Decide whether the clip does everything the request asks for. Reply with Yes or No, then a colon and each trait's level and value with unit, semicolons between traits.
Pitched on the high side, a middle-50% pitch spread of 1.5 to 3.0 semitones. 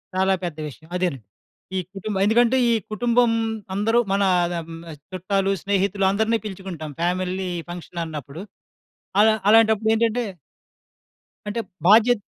No: high, 195 Hz; average, 3.8 semitones